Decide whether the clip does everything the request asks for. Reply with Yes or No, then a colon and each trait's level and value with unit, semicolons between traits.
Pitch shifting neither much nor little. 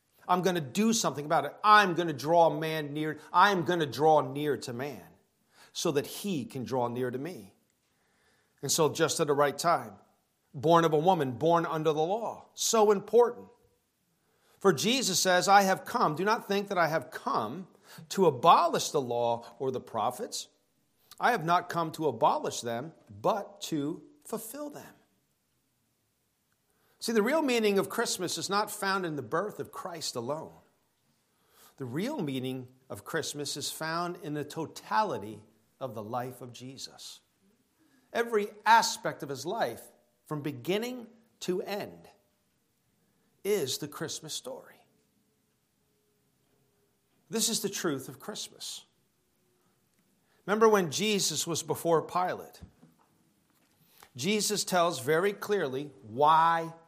No: wide, 6.0 semitones